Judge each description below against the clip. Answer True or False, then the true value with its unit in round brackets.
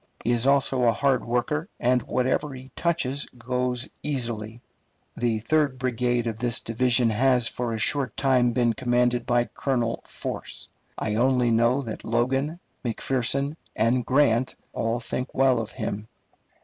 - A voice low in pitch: True (125 Hz)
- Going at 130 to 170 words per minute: True (150 wpm)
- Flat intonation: True (2.1 semitones)